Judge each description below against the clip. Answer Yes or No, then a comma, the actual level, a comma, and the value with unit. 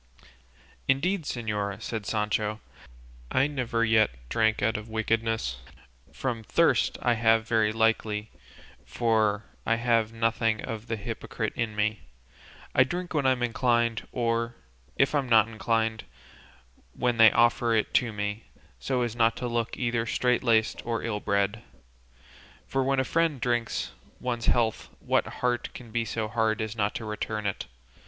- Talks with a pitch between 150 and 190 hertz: No, low, 115 Hz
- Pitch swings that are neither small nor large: No, narrow, 1.8 semitones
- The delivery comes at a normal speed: Yes, average, 155 wpm